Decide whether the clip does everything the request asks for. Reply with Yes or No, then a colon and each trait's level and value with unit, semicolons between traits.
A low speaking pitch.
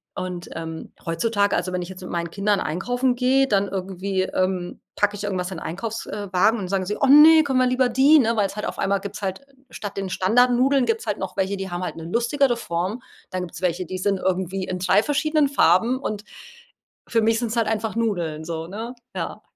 No: high, 200 Hz